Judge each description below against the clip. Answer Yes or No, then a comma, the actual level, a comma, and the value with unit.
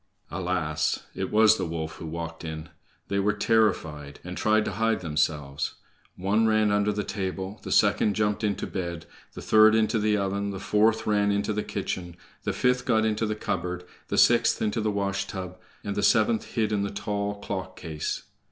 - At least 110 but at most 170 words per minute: No, average, 185 wpm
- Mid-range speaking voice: No, low, 100 Hz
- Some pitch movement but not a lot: Yes, average, 3.1 semitones